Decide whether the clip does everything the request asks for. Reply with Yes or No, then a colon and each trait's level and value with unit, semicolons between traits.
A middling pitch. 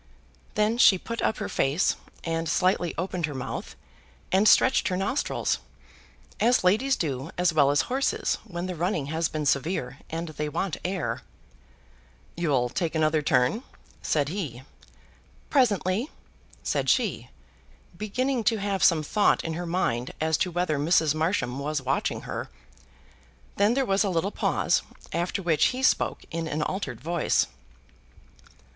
Yes: medium, 170 Hz